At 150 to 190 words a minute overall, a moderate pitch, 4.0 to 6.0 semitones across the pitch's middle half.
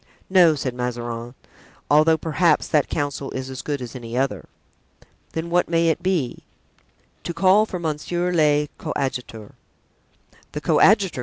No: average, 140 wpm; medium, 150 Hz; average, 4.9 semitones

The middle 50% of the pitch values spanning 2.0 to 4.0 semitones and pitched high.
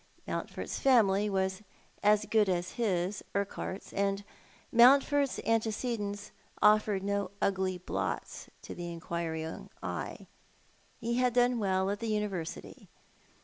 Yes: average, 3.1 semitones; high, 200 Hz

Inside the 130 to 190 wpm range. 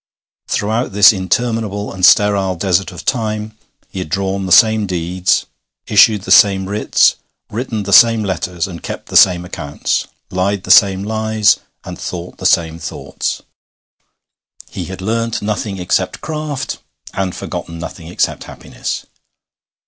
Yes: average, 140 wpm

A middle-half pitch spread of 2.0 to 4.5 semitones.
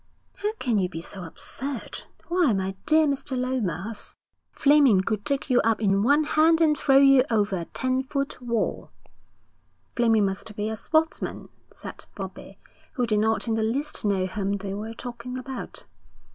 No: average, 5.1 semitones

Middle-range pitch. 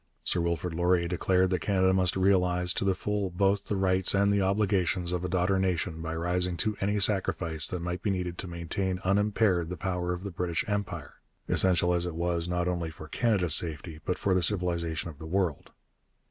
No: very low, 90 Hz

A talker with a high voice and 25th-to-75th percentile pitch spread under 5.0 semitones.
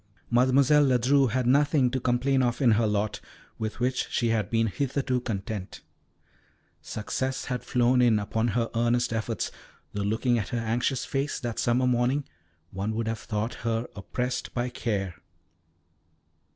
No: low, 120 Hz; narrow, 2.4 semitones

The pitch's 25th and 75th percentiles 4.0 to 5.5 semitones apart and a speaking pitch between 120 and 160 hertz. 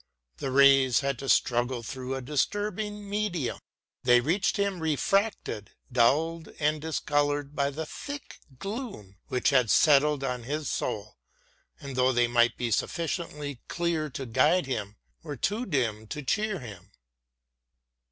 Yes: average, 5.1 semitones; medium, 140 Hz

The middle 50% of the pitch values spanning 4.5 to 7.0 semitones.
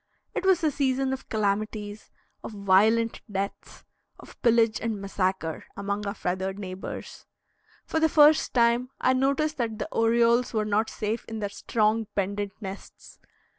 No: average, 3.2 semitones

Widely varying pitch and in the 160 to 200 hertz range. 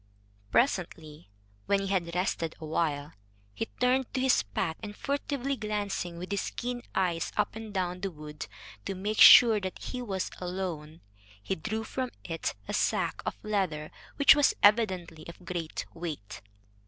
No: average, 4.7 semitones; high, 190 Hz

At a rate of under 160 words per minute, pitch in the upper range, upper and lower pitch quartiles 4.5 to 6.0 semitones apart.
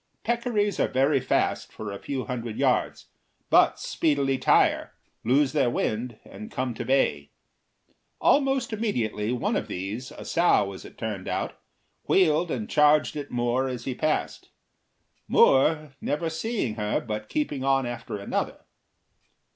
No: average, 145 wpm; low, 130 Hz; average, 5.1 semitones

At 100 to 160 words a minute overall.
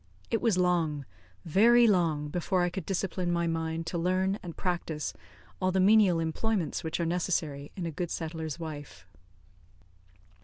Yes: average, 155 wpm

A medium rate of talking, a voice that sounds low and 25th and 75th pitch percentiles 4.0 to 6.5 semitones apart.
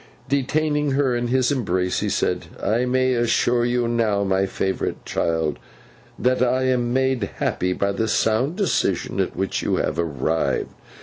Yes: average, 160 wpm; low, 120 Hz; average, 4.7 semitones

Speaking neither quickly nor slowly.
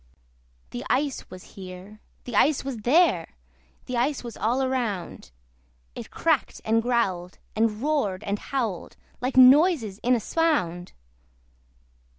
No: slow, 130 wpm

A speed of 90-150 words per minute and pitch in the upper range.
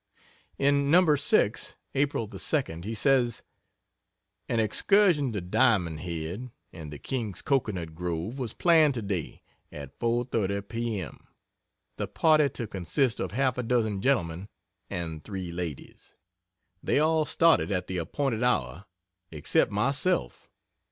No: slow, 135 wpm; low, 110 Hz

